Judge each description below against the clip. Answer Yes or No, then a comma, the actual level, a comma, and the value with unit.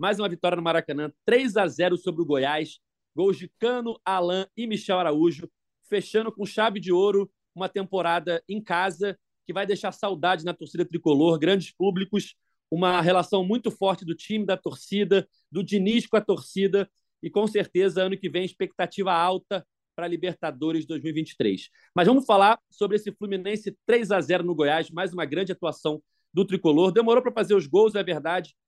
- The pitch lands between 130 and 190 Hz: Yes, medium, 185 Hz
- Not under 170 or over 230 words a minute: Yes, average, 180 wpm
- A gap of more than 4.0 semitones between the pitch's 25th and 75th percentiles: No, average, 2.9 semitones